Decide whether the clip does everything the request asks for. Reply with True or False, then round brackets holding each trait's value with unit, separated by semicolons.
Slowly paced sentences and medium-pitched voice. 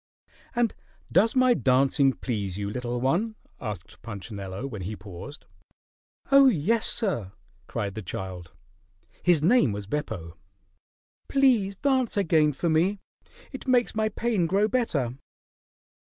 True (125 wpm; 150 Hz)